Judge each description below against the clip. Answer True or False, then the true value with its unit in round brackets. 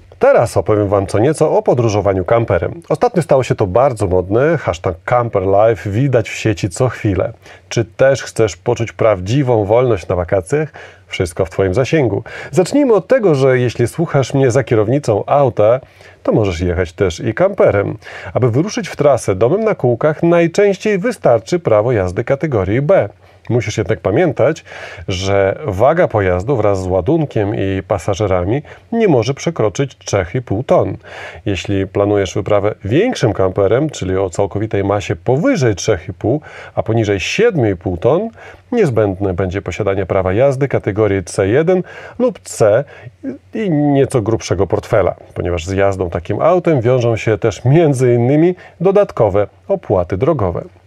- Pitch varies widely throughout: True (6.1 semitones)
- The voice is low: True (110 Hz)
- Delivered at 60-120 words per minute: False (140 wpm)